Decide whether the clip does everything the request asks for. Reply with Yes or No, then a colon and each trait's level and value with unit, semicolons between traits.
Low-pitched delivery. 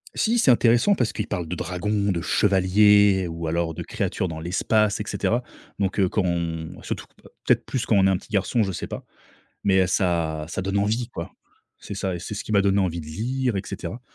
Yes: very low, 95 Hz